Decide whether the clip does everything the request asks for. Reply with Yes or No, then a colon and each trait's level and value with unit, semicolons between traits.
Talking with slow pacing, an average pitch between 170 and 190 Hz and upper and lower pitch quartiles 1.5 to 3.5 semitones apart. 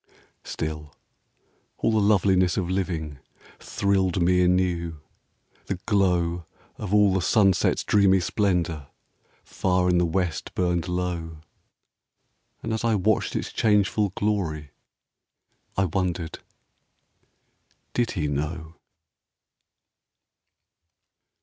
No: slow, 105 wpm; very low, 90 Hz; average, 2.7 semitones